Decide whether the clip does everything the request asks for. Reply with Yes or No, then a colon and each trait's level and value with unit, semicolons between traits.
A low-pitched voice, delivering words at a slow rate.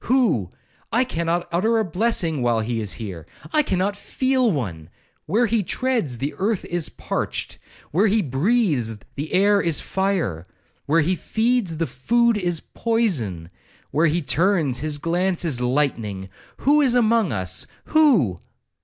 No: medium, 170 Hz; slow, 130 wpm